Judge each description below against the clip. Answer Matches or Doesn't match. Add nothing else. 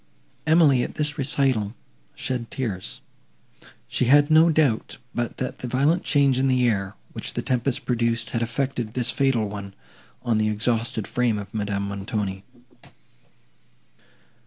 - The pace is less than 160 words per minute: Matches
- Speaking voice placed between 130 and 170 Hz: Doesn't match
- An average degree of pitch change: Matches